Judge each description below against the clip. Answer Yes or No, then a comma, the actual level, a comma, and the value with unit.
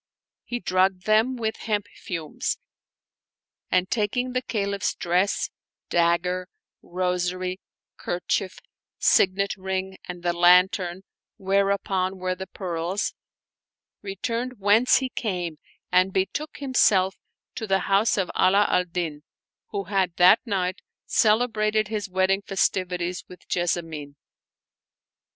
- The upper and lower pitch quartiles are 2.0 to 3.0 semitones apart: Yes, narrow, 2.4 semitones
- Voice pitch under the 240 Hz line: Yes, high, 190 Hz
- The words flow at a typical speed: No, slow, 115 wpm